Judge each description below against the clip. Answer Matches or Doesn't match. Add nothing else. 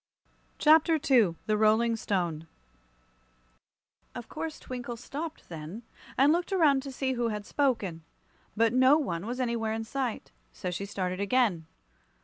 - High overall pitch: Matches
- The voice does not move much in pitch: Doesn't match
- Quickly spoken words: Doesn't match